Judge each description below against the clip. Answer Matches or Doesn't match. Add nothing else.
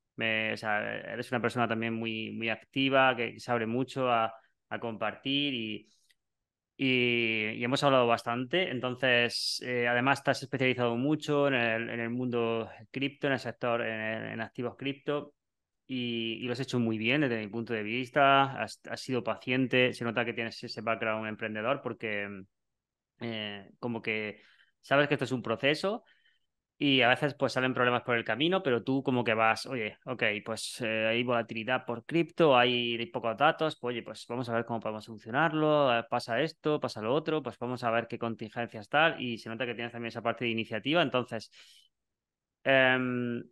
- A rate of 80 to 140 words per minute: Doesn't match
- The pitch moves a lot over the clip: Doesn't match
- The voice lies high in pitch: Doesn't match